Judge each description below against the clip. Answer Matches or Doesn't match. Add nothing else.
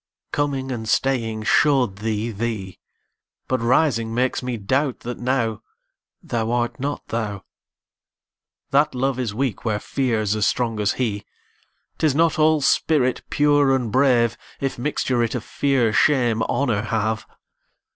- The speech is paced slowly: Matches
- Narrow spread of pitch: Doesn't match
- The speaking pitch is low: Matches